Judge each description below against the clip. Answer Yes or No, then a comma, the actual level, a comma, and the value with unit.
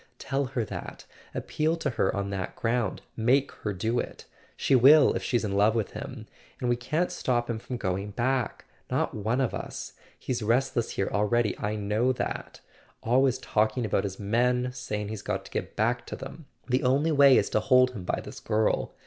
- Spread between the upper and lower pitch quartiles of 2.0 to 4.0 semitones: Yes, average, 3.5 semitones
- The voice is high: No, low, 120 Hz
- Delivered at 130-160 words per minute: No, average, 190 wpm